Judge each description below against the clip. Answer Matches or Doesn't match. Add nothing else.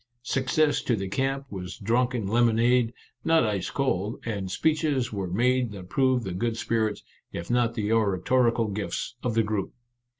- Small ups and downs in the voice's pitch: Doesn't match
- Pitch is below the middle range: Matches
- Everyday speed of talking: Matches